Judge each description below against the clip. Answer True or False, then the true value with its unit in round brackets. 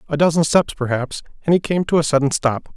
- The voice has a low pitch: False (150 Hz)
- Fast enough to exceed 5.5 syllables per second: True (6.1 syllables/s)